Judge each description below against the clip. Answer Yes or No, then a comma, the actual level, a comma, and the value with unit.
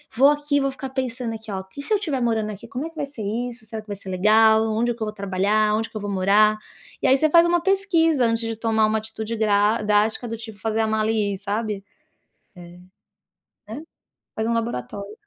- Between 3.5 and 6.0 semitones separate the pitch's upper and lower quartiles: No, average, 3.0 semitones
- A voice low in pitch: No, high, 220 Hz